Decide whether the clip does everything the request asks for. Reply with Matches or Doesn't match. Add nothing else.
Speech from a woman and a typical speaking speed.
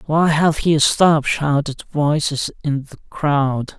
Doesn't match